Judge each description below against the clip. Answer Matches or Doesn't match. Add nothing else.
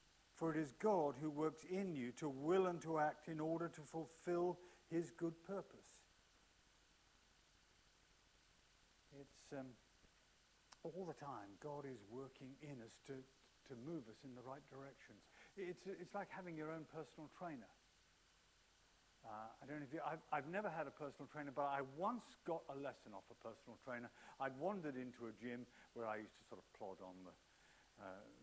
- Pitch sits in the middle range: Matches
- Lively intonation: Doesn't match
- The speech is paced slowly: Doesn't match